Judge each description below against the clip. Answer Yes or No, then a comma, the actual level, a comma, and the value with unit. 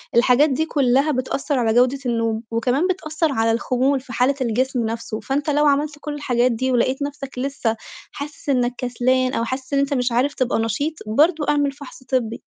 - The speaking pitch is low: No, very high, 260 Hz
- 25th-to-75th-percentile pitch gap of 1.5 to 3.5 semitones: Yes, average, 2.9 semitones